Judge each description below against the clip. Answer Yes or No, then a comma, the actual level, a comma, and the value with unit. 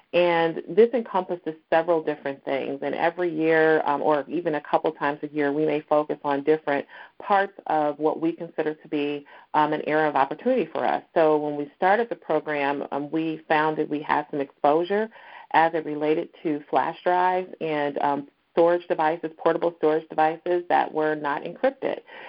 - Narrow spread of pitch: Yes, narrow, 2.3 semitones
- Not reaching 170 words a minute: No, average, 180 wpm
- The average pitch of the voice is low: No, medium, 155 Hz